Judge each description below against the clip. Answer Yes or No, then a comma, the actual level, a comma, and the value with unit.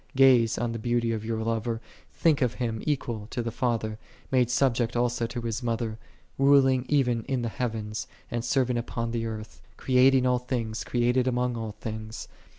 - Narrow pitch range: Yes, narrow, 1.9 semitones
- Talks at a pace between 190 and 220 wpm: No, average, 180 wpm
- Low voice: Yes, low, 120 Hz